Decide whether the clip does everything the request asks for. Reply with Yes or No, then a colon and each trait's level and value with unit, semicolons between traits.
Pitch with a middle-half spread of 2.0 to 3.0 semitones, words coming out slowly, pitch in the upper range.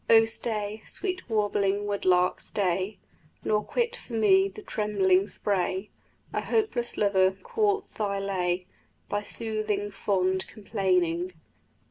Yes: narrow, 2.5 semitones; slow, 120 wpm; high, 205 Hz